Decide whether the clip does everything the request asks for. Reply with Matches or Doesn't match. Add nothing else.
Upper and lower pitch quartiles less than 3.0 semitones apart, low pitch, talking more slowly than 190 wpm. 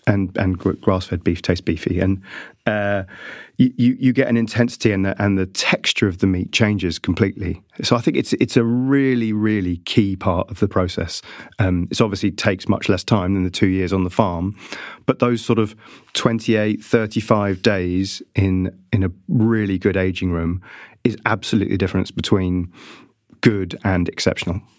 Doesn't match